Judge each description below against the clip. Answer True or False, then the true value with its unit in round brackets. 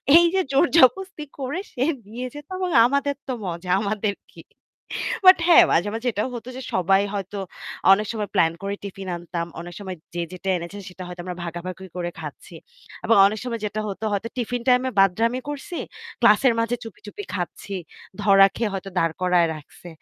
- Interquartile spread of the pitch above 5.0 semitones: True (5.4 semitones)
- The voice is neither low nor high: False (205 Hz)